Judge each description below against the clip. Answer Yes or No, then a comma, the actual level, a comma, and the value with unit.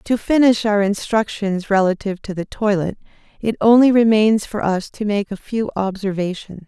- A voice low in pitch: No, high, 205 Hz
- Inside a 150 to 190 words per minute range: Yes, average, 160 wpm